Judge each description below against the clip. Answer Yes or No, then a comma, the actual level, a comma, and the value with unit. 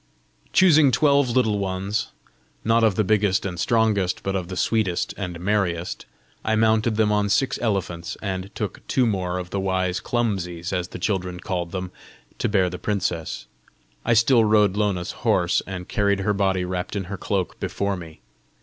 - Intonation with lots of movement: No, average, 3.0 semitones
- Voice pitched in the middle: No, low, 100 Hz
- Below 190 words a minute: Yes, average, 175 wpm